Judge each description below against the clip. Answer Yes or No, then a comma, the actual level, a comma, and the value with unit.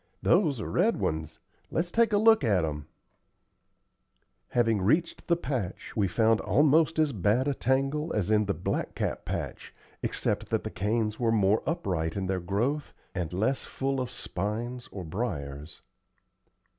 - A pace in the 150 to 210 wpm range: Yes, average, 155 wpm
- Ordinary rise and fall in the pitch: No, wide, 6.6 semitones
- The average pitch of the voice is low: Yes, low, 115 Hz